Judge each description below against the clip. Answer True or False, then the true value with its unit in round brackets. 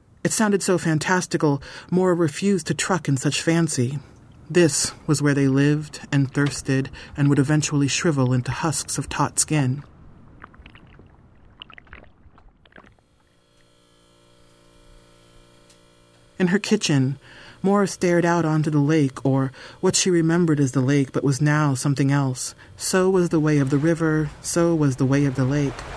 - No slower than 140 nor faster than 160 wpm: True (145 wpm)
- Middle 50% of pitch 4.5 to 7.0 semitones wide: False (3.9 semitones)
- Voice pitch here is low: False (145 Hz)